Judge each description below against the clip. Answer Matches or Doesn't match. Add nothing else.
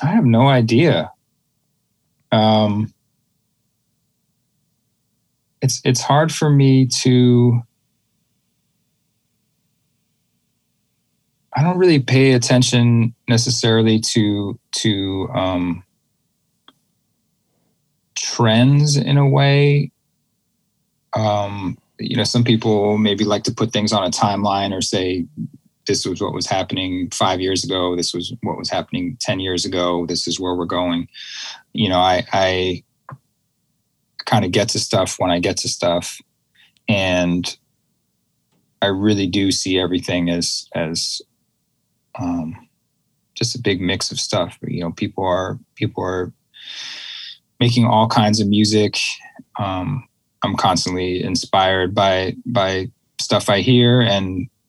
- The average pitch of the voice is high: Doesn't match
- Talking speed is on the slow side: Matches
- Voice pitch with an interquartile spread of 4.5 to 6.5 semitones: Matches